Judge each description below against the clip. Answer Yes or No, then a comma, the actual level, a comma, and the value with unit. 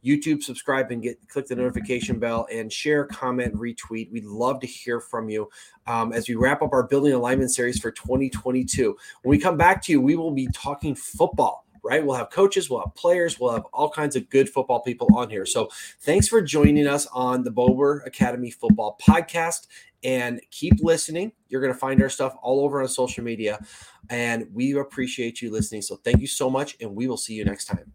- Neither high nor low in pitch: No, low, 130 Hz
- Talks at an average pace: No, fast, 215 wpm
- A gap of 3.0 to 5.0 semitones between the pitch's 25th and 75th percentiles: Yes, average, 3.5 semitones